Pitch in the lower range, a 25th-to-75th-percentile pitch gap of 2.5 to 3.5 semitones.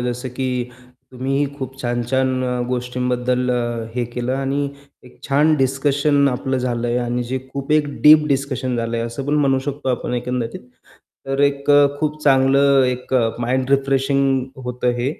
No: low, 130 Hz; narrow, 1.9 semitones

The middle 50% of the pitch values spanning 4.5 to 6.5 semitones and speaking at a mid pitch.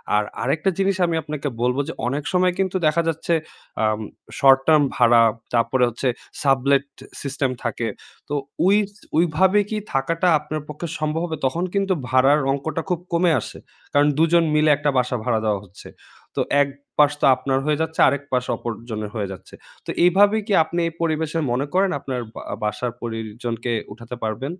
Yes: average, 5.0 semitones; medium, 145 Hz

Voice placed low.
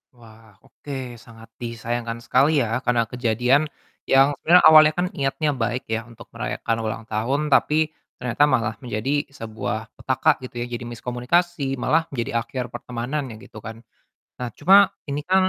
Yes: low, 125 Hz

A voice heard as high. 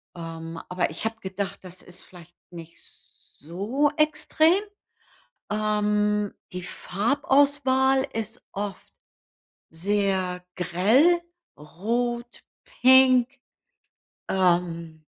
Yes: high, 205 Hz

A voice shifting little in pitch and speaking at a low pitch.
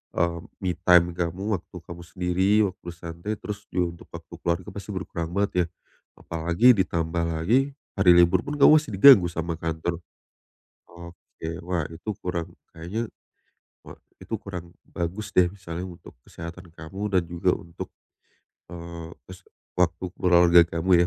Yes: narrow, 1.9 semitones; very low, 85 Hz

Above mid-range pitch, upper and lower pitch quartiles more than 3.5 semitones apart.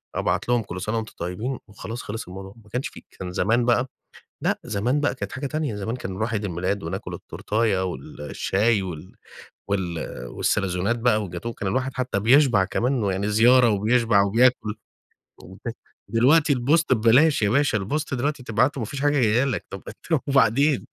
No: low, 115 Hz; average, 4.4 semitones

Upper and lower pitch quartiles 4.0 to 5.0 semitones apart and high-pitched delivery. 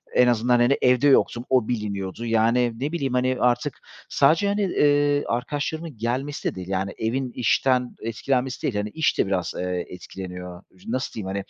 No: average, 4.5 semitones; low, 120 Hz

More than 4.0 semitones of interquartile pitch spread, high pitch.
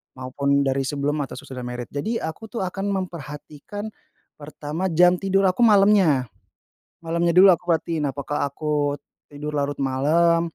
No: average, 4.4 semitones; medium, 155 Hz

